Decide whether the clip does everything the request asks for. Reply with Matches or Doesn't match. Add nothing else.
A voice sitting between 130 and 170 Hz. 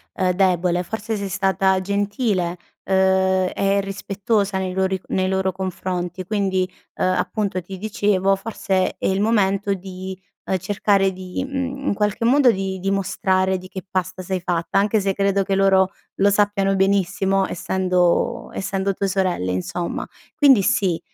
Doesn't match